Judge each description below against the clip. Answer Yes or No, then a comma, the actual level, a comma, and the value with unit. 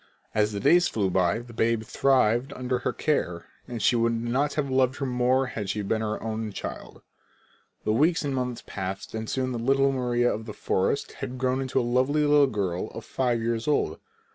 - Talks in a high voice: No, low, 120 Hz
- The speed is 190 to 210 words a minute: Yes, average, 200 wpm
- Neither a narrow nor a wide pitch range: Yes, average, 3.2 semitones